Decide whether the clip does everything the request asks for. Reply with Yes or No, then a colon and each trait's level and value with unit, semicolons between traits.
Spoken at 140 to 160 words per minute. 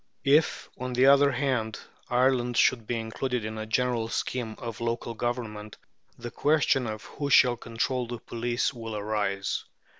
Yes: average, 155 wpm